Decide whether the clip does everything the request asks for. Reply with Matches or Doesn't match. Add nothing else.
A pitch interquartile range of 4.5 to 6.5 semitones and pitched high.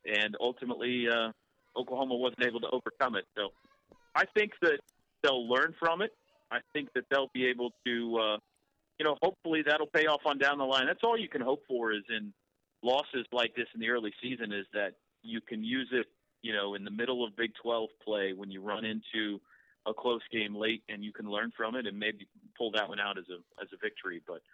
Doesn't match